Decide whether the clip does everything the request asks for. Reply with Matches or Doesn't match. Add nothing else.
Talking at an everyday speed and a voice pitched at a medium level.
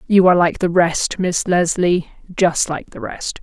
Matches